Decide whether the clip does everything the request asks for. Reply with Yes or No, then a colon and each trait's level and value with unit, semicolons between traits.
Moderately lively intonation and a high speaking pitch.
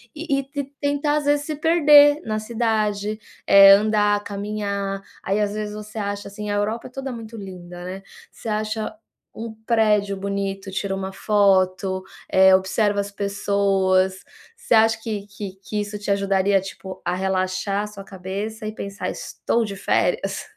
No: narrow, 2.1 semitones; high, 205 Hz